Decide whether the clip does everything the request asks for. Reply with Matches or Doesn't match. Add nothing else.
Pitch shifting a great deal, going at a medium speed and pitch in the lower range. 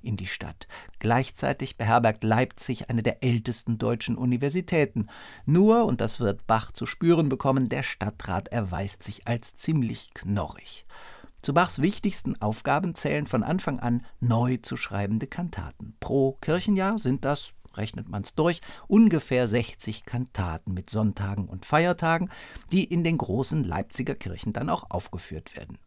Matches